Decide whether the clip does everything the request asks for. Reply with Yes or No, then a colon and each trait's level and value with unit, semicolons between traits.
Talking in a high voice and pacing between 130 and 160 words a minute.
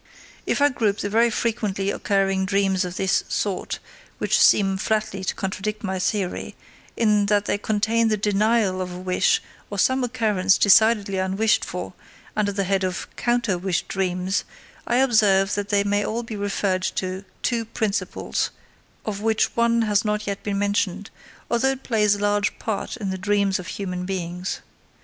No: high, 205 Hz; average, 170 wpm